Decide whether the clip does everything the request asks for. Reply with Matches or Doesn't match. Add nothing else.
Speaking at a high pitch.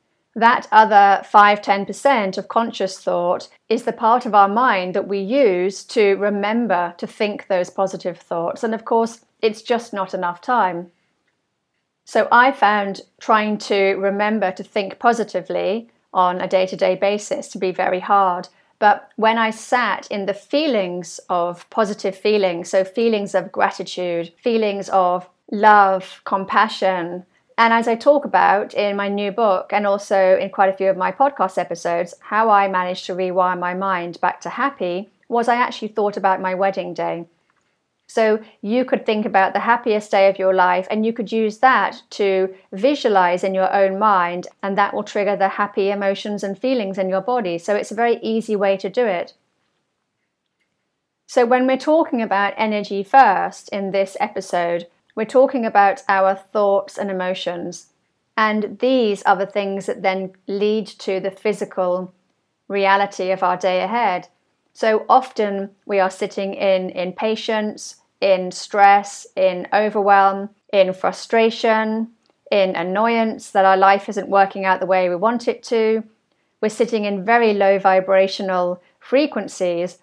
Matches